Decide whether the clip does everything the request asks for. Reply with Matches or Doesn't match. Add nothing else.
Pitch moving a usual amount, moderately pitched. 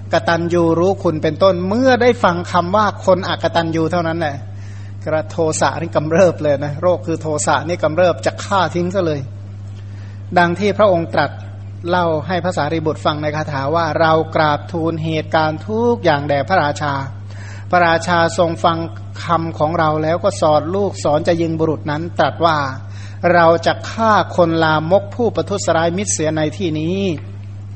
Matches